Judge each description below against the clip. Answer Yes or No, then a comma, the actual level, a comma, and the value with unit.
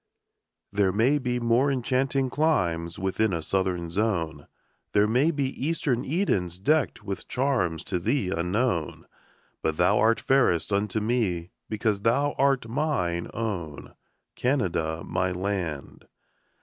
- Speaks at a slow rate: Yes, slow, 125 wpm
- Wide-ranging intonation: Yes, wide, 6.5 semitones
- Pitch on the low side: Yes, low, 105 Hz